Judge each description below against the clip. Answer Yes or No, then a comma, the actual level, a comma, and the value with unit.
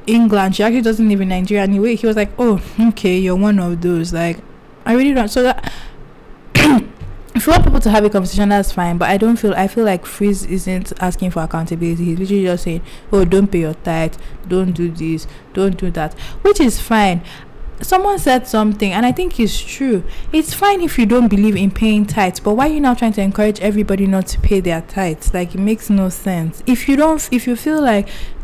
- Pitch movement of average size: Yes, average, 3.9 semitones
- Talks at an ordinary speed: No, fast, 225 wpm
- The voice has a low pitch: No, high, 200 Hz